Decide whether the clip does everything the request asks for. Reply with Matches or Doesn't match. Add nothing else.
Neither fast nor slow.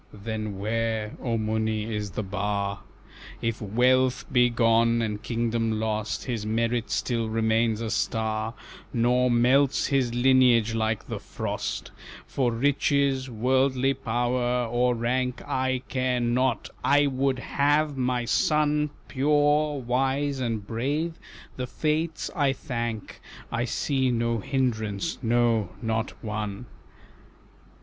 Doesn't match